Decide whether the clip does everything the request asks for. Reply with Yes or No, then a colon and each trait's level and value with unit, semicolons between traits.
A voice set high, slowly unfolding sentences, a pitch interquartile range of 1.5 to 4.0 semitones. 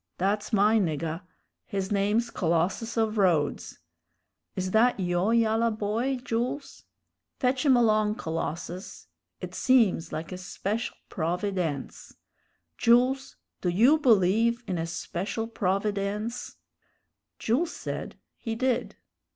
No: high, 210 Hz; slow, 110 wpm; average, 4.4 semitones